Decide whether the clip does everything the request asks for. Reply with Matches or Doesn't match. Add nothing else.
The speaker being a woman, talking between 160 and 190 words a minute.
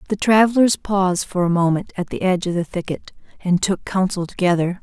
Doesn't match